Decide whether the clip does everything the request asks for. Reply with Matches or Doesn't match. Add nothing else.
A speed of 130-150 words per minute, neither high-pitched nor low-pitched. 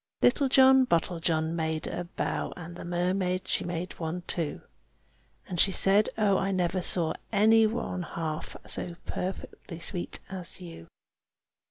Matches